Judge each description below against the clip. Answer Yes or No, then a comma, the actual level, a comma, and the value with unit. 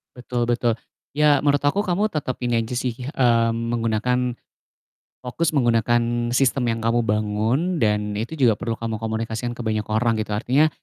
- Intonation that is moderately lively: No, narrow, 2.2 semitones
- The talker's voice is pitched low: Yes, low, 120 Hz